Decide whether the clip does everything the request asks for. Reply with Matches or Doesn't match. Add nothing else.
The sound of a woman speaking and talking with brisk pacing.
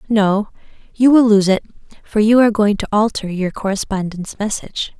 Doesn't match